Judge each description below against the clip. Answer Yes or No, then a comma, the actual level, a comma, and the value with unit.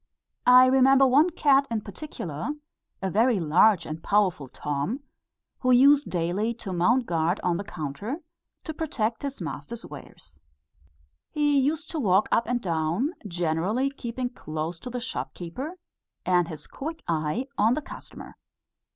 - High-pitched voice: Yes, high, 220 Hz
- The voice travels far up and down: Yes, wide, 7.7 semitones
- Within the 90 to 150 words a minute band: Yes, average, 145 wpm